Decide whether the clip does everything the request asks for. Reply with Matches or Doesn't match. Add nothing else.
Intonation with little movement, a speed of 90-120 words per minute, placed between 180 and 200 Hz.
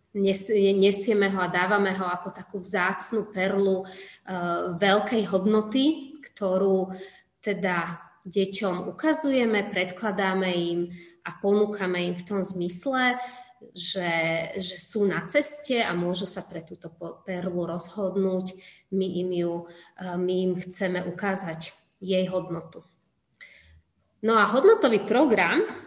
Matches